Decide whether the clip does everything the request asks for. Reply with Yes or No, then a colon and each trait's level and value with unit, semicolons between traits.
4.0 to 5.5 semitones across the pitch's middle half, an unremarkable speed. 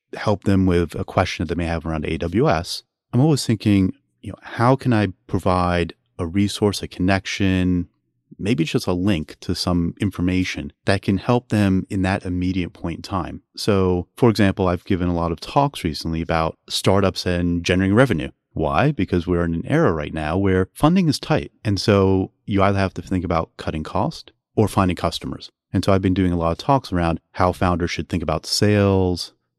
No: narrow, 2.5 semitones; average, 195 wpm